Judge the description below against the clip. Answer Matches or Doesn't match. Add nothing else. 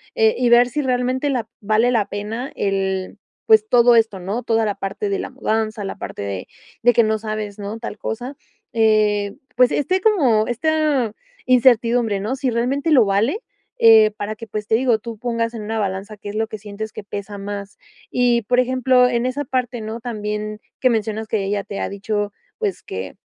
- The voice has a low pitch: Doesn't match